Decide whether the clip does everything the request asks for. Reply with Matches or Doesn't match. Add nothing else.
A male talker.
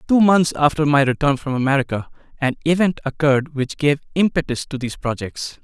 Matches